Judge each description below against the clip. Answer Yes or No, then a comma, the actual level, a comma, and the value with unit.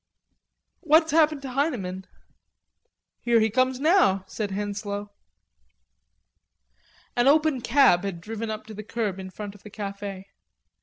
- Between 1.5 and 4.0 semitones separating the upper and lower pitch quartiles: No, average, 5.2 semitones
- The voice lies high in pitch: Yes, high, 220 Hz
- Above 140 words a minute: No, slow, 135 wpm